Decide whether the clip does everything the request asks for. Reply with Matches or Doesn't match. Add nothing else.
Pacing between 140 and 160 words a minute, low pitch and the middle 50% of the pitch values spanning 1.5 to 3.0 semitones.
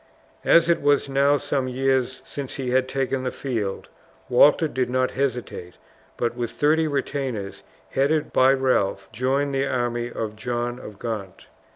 Matches